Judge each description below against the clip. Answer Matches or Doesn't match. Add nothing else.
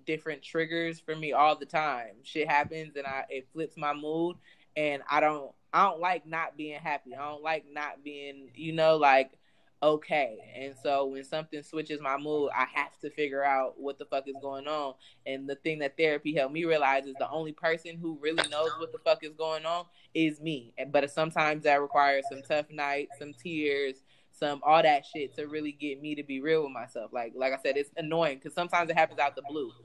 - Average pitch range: Doesn't match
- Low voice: Doesn't match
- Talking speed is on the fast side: Matches